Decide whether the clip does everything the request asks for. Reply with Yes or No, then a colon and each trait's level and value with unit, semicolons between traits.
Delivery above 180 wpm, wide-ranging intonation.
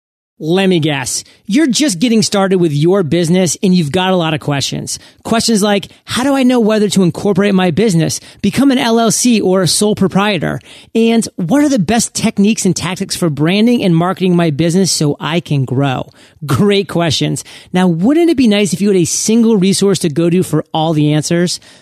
No: average, 200 wpm; average, 4.5 semitones